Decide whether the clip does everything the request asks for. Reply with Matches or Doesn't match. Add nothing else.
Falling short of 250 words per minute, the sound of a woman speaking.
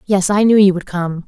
Doesn't match